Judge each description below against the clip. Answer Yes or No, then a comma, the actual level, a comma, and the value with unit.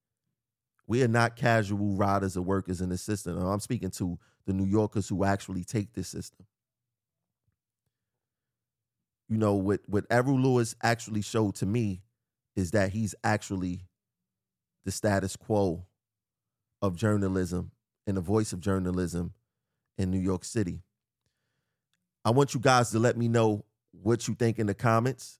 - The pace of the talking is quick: No, average, 150 wpm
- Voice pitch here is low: Yes, low, 110 Hz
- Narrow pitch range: No, average, 3.4 semitones